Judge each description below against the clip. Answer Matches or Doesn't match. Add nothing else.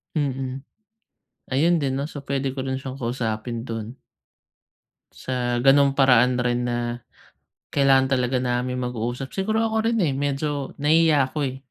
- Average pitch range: Doesn't match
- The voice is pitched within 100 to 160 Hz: Matches